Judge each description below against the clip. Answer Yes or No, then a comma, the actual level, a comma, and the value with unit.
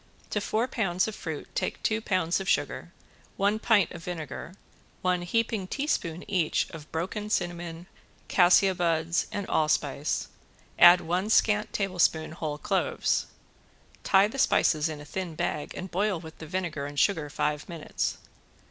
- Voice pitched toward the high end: No, medium, 175 Hz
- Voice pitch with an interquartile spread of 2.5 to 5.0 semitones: Yes, average, 3.7 semitones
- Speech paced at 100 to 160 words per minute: Yes, average, 150 wpm